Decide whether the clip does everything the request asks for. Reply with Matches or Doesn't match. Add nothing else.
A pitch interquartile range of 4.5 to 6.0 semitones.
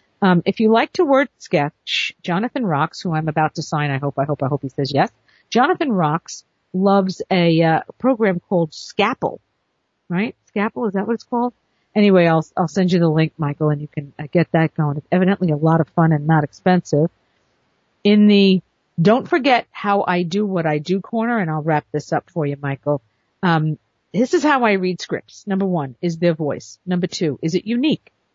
Matches